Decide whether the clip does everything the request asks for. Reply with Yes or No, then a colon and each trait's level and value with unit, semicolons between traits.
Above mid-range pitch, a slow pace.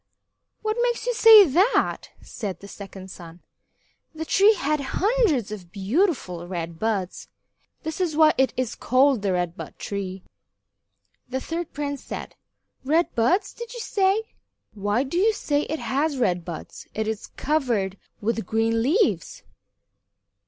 No: very high, 260 Hz; average, 145 wpm